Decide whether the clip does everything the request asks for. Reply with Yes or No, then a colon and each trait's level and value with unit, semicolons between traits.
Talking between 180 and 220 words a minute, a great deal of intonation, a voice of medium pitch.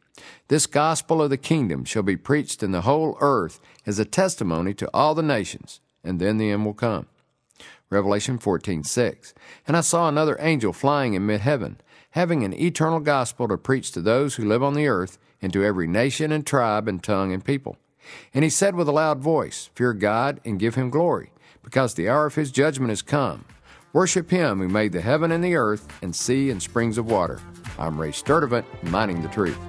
No: fast, 205 wpm; wide, 6.9 semitones; low, 125 Hz